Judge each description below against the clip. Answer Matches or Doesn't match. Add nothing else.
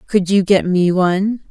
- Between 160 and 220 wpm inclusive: Matches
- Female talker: Matches